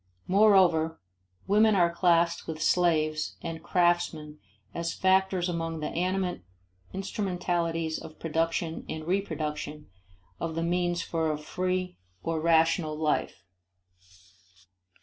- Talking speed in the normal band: No, slow, 110 wpm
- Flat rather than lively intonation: Yes, narrow, 2.1 semitones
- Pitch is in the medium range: Yes, medium, 170 Hz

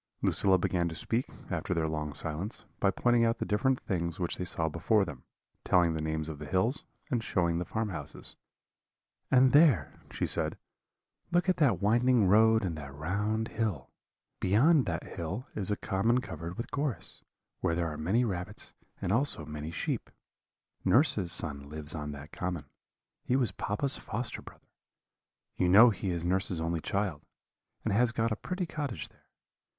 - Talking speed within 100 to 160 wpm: No, average, 175 wpm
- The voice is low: Yes, very low, 95 Hz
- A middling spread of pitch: No, wide, 5.9 semitones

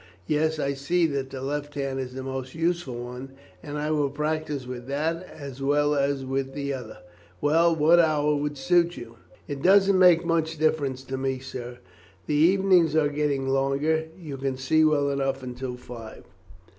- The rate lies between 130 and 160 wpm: No, average, 180 wpm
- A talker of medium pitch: Yes, medium, 145 Hz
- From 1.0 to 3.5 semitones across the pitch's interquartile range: Yes, average, 2.9 semitones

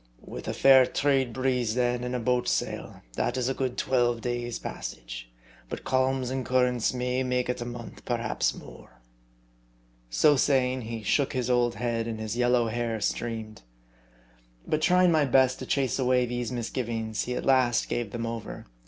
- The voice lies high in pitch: No, low, 125 Hz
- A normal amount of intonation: No, narrow, 1.8 semitones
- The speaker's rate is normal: Yes, average, 175 wpm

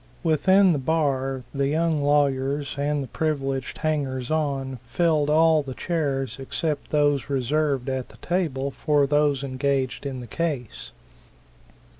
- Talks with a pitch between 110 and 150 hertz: Yes, medium, 140 Hz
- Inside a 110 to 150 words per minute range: Yes, slow, 135 wpm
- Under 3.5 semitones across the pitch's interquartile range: Yes, narrow, 2.5 semitones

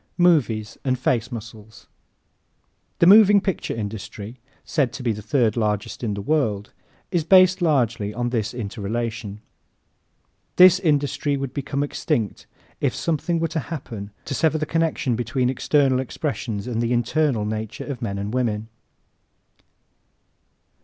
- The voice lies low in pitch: Yes, low, 125 Hz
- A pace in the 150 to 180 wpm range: No, average, 140 wpm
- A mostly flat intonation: No, wide, 5.5 semitones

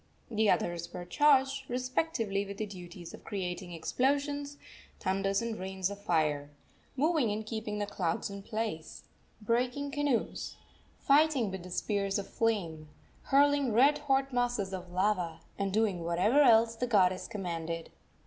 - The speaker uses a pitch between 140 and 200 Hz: No, high, 210 Hz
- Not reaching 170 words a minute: Yes, average, 140 wpm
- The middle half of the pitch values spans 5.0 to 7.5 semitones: Yes, wide, 5.6 semitones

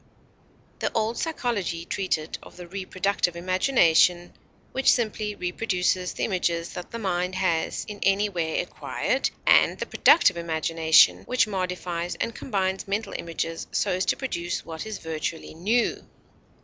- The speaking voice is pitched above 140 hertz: Yes, medium, 185 Hz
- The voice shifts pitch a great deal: No, average, 3.5 semitones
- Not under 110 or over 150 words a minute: Yes, average, 140 wpm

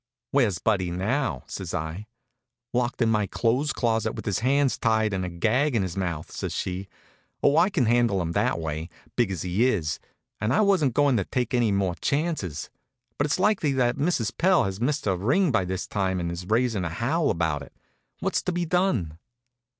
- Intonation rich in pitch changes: Yes, wide, 7.0 semitones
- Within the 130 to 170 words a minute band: No, average, 200 wpm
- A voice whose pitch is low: Yes, low, 110 Hz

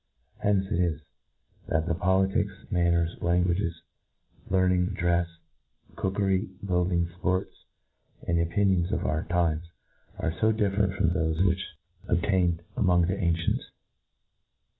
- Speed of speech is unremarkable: No, slow, 115 wpm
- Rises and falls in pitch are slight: Yes, narrow, 2.1 semitones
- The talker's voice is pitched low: Yes, very low, 90 Hz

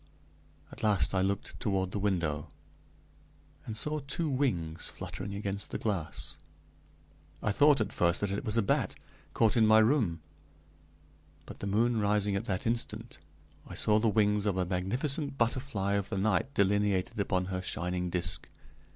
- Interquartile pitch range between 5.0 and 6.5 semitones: No, average, 3.2 semitones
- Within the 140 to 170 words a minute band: Yes, average, 160 wpm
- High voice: No, low, 100 Hz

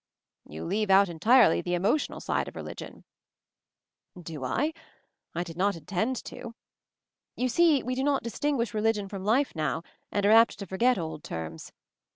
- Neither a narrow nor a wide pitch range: No, wide, 6.2 semitones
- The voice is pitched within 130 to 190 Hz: No, high, 205 Hz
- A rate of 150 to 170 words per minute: Yes, average, 165 wpm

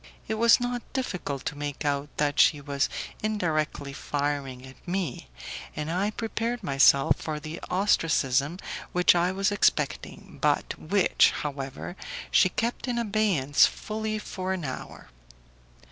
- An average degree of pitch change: No, wide, 6.5 semitones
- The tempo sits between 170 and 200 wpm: No, slow, 135 wpm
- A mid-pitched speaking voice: Yes, medium, 165 Hz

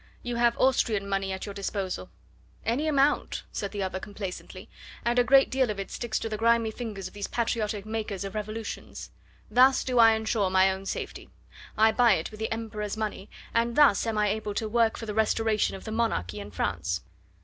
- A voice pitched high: Yes, high, 215 Hz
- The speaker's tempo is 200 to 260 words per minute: Yes, fast, 205 wpm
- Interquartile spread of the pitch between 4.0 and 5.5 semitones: No, average, 2.7 semitones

